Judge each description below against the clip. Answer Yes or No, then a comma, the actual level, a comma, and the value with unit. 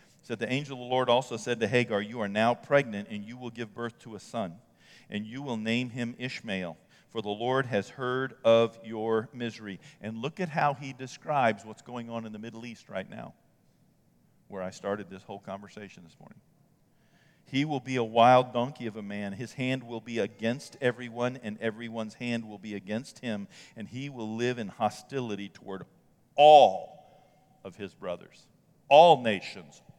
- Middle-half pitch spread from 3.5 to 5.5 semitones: No, average, 3.0 semitones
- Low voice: Yes, low, 120 Hz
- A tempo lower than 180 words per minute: No, average, 190 wpm